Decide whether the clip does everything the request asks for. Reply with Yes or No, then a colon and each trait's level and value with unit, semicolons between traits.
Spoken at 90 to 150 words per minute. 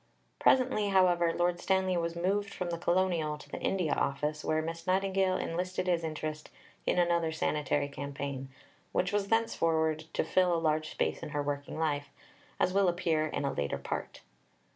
No: average, 170 wpm